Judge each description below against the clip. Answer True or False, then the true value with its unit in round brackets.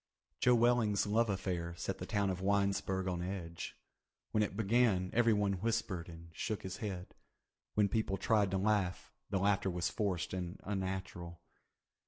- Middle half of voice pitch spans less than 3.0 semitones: True (2.5 semitones)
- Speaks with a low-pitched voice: True (95 Hz)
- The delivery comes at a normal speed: True (155 wpm)